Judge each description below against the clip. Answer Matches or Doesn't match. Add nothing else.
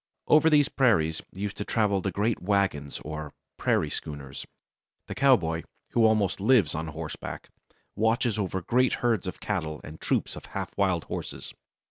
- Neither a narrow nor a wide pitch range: Doesn't match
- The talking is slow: Doesn't match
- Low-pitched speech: Matches